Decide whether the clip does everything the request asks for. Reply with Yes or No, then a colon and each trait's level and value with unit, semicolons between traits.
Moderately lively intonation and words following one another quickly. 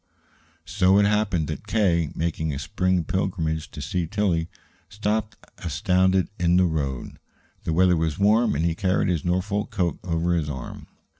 No: average, 3.2 semitones; average, 160 wpm